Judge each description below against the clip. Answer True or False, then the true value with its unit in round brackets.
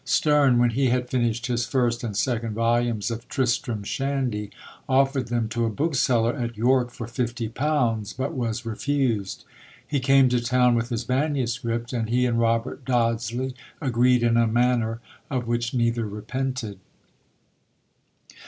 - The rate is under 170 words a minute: True (150 wpm)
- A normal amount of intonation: False (1.9 semitones)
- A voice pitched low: True (120 Hz)